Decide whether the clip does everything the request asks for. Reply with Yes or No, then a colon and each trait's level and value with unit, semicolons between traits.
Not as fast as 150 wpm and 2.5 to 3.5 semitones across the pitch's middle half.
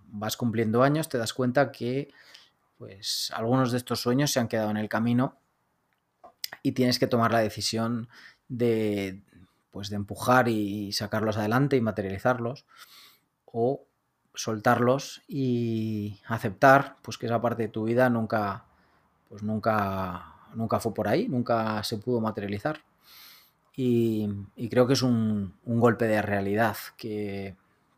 Yes: average, 140 wpm; average, 2.8 semitones